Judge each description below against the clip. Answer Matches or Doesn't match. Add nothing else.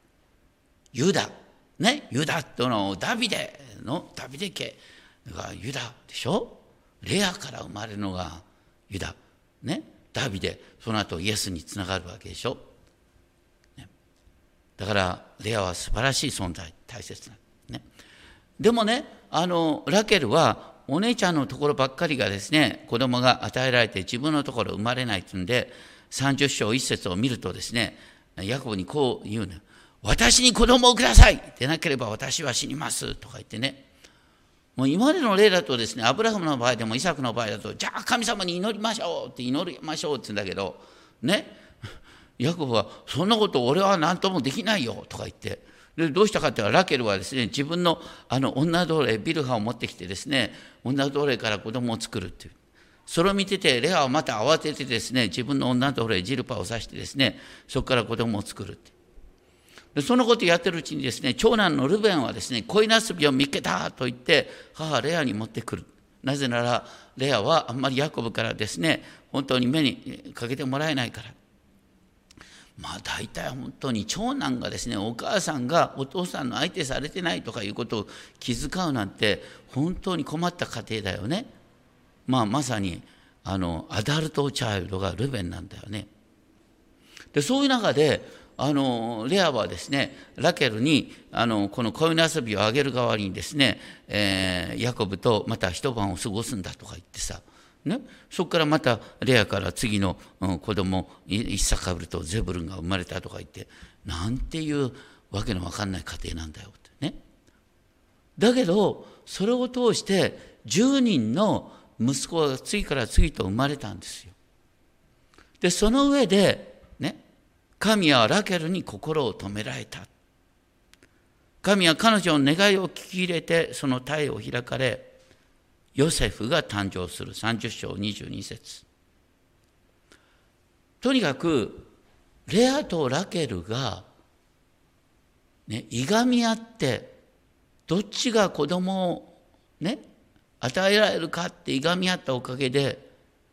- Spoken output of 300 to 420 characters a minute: Matches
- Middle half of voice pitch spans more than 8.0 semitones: Matches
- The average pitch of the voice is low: Matches